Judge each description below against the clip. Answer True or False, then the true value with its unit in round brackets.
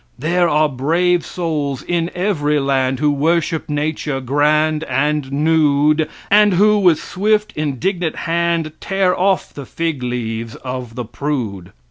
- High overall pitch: False (155 Hz)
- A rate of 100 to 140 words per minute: True (135 wpm)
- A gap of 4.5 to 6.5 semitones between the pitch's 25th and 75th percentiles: False (3.8 semitones)